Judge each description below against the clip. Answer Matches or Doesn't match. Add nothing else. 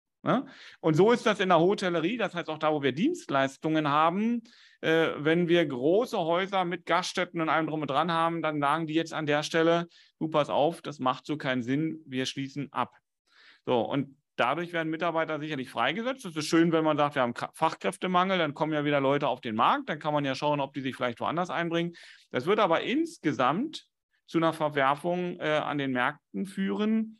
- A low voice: Doesn't match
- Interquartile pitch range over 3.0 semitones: Matches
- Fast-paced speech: Matches